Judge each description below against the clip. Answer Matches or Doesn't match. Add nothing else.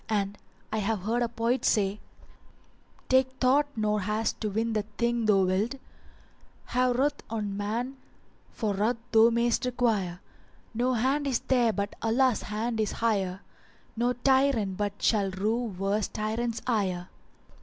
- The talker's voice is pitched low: Doesn't match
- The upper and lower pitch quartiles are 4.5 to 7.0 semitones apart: Doesn't match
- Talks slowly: Doesn't match